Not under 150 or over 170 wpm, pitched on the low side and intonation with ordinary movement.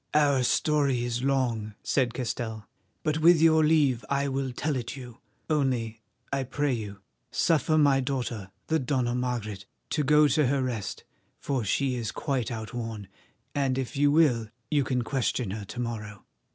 Yes: average, 160 wpm; low, 130 Hz; average, 3.6 semitones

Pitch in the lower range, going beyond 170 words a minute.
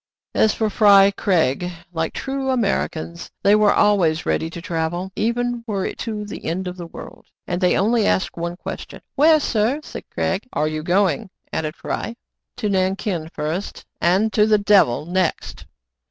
No: high, 195 Hz; average, 185 wpm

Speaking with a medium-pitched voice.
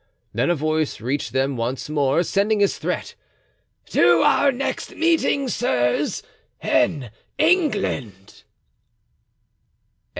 Yes: medium, 155 Hz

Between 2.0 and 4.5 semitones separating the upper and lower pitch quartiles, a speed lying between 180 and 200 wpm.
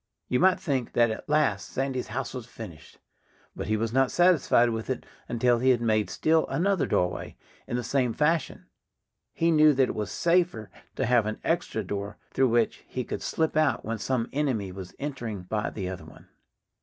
No: average, 5.1 semitones; average, 195 wpm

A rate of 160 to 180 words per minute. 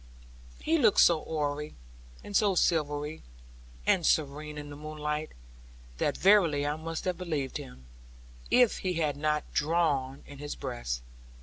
No: average, 140 wpm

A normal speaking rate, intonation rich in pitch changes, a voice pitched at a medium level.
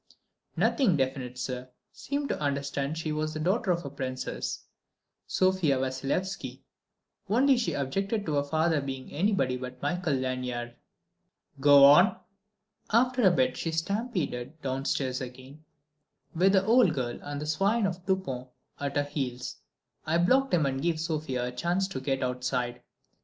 Yes: average, 150 wpm; wide, 6.2 semitones; medium, 150 Hz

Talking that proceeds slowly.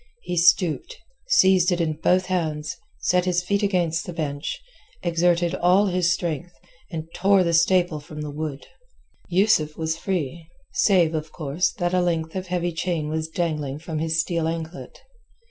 No: average, 165 wpm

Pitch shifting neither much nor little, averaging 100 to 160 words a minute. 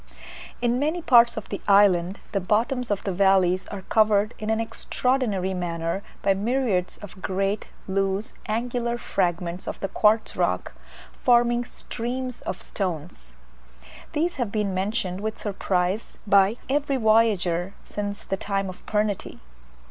Yes: average, 3.7 semitones; average, 140 wpm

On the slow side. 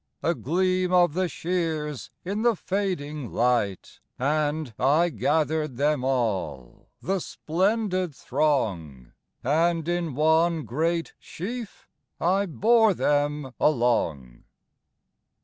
Yes: slow, 90 wpm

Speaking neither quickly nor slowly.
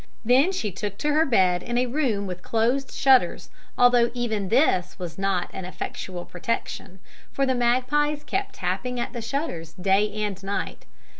Yes: average, 165 wpm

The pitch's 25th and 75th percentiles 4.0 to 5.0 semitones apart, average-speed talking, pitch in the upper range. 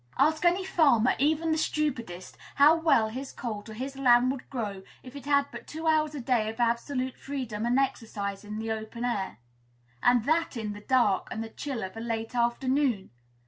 Yes: average, 4.3 semitones; average, 195 wpm; high, 245 Hz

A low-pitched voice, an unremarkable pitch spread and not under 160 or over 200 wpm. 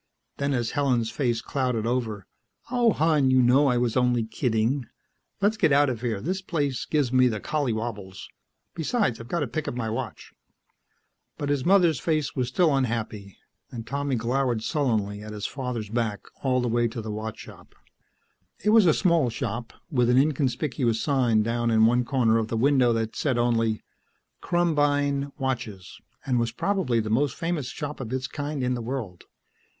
Yes: low, 125 Hz; average, 4.0 semitones; average, 180 wpm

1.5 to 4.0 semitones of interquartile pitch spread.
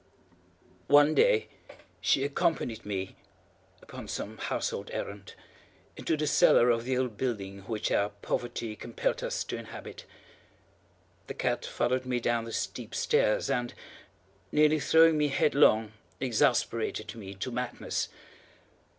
No: average, 4.6 semitones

